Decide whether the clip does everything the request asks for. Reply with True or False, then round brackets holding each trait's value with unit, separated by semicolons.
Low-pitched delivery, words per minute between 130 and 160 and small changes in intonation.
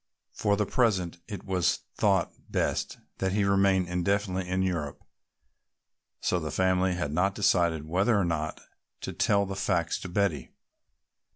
True (95 Hz; 150 wpm; 2.3 semitones)